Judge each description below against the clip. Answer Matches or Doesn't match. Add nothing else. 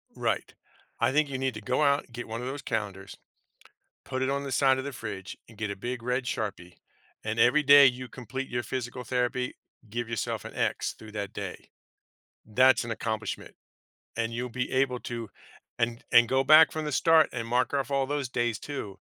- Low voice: Matches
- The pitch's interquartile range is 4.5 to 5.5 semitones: Doesn't match